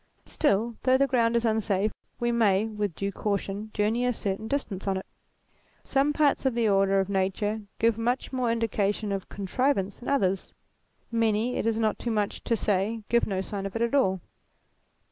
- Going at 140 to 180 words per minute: No, average, 190 wpm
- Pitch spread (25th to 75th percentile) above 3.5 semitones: No, average, 3.1 semitones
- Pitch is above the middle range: Yes, high, 220 Hz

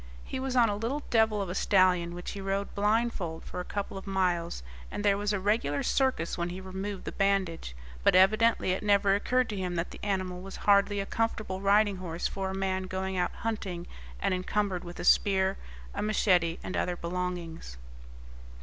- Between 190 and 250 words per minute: Yes, average, 195 wpm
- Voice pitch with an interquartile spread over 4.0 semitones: No, narrow, 2.4 semitones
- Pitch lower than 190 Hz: No, high, 195 Hz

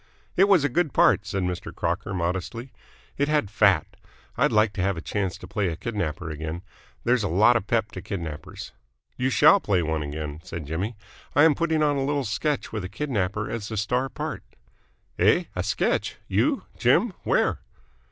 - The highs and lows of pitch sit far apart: Yes, wide, 6.0 semitones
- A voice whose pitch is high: No, low, 105 Hz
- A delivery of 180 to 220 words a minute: Yes, average, 190 wpm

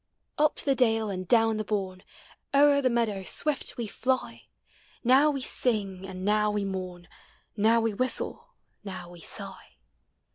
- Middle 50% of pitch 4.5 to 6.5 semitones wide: Yes, average, 4.8 semitones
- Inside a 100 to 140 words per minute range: No, average, 150 wpm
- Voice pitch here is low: No, high, 215 Hz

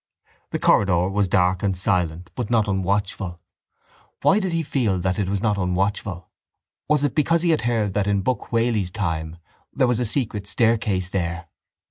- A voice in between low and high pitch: No, low, 100 Hz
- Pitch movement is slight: No, average, 4.4 semitones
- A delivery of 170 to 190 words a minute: Yes, average, 175 wpm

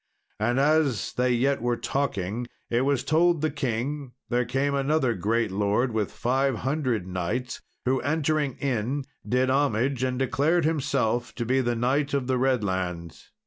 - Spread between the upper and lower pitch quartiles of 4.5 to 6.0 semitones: No, average, 3.1 semitones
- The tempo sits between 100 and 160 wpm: Yes, average, 155 wpm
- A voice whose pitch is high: No, low, 130 Hz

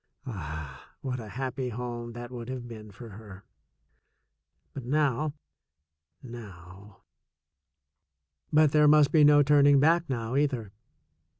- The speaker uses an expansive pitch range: No, average, 4.8 semitones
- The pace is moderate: No, slow, 120 wpm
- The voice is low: Yes, low, 125 Hz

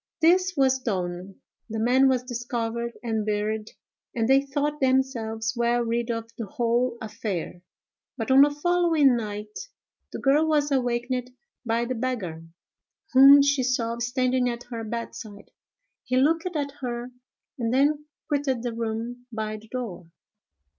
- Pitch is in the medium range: No, high, 245 Hz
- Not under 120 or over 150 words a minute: Yes, average, 145 wpm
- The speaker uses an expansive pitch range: No, average, 3.0 semitones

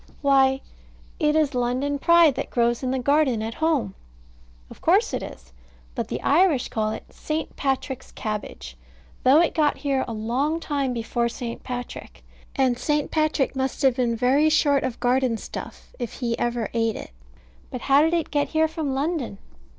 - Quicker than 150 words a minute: Yes, average, 175 wpm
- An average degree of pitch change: Yes, average, 3.8 semitones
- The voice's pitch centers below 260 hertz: No, very high, 265 Hz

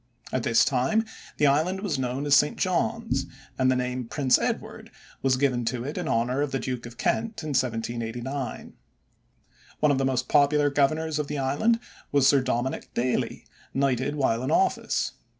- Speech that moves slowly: No, average, 175 wpm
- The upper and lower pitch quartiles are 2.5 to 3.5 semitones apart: Yes, average, 2.8 semitones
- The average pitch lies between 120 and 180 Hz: Yes, low, 135 Hz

